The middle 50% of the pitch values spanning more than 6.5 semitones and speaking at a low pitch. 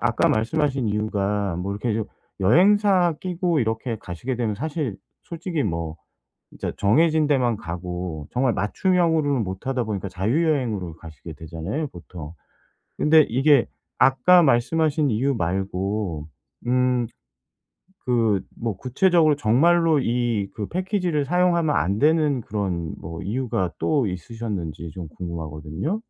Yes: wide, 8.3 semitones; low, 115 Hz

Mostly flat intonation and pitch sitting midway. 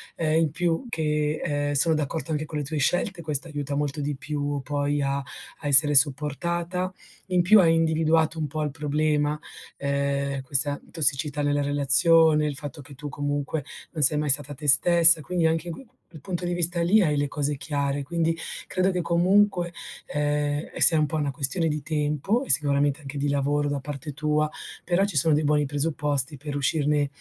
Yes: narrow, 2.2 semitones; medium, 150 Hz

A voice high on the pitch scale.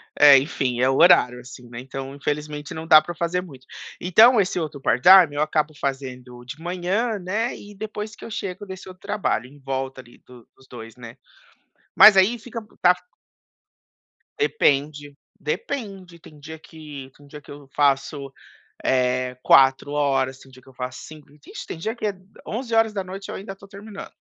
No: medium, 150 Hz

